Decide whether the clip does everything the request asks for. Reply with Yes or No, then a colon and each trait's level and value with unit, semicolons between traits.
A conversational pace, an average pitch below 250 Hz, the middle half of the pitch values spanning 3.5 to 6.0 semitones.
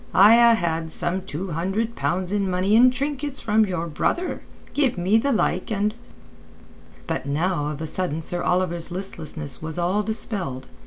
Yes: average, 165 wpm; medium, 185 Hz; average, 4.8 semitones